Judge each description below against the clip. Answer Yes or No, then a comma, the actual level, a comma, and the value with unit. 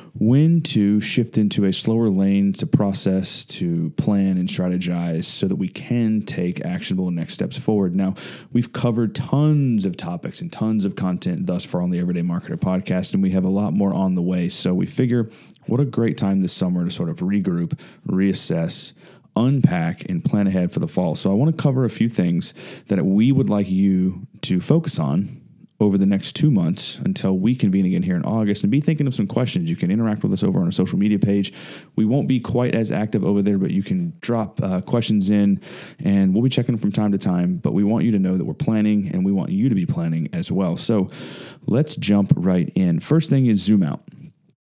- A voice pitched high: No, low, 110 Hz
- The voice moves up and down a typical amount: No, wide, 8.9 semitones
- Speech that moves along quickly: Yes, fast, 225 wpm